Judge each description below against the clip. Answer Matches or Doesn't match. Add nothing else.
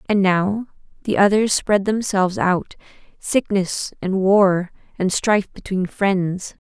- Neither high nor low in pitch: Doesn't match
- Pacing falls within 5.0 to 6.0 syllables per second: Doesn't match